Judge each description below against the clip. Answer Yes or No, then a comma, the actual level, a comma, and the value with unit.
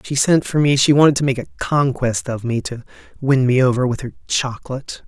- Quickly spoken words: Yes, fast, 225 wpm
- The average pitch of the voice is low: Yes, low, 130 Hz